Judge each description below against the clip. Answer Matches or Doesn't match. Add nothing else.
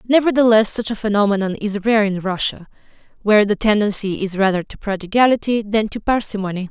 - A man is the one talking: Doesn't match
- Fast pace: Doesn't match